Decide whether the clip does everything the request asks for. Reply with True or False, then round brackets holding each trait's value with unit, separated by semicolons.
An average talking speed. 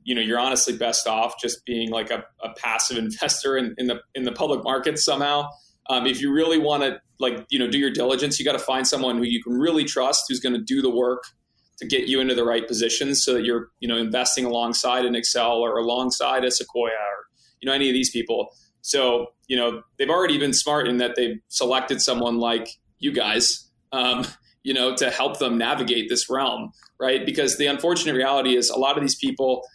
False (225 wpm)